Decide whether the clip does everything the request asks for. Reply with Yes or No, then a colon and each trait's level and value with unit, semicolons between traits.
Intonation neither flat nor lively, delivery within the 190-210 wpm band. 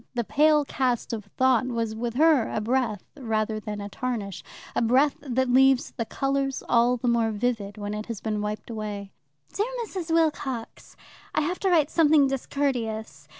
No: average, 4.1 semitones; average, 175 wpm